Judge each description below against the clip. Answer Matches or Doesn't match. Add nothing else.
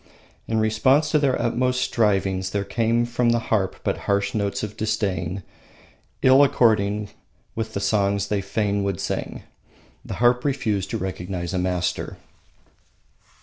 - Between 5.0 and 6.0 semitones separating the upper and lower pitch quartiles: Doesn't match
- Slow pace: Doesn't match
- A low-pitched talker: Matches